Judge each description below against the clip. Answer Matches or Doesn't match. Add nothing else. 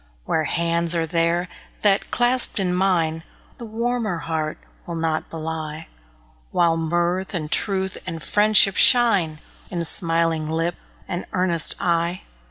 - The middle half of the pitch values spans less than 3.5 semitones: Matches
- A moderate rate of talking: Doesn't match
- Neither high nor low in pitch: Matches